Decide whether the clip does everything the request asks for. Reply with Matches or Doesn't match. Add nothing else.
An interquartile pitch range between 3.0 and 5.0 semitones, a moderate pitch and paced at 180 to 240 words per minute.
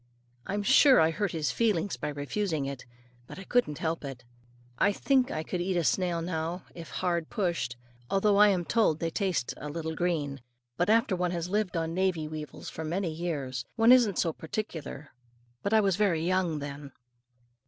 Matches